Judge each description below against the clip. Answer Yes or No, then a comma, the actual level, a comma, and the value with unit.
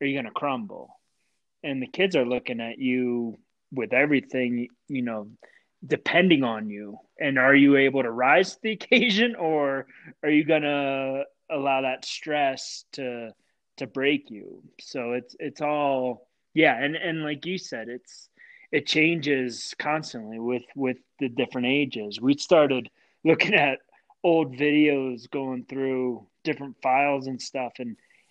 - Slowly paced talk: No, average, 150 wpm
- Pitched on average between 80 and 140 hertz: Yes, low, 135 Hz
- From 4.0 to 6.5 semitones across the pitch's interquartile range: No, average, 3.1 semitones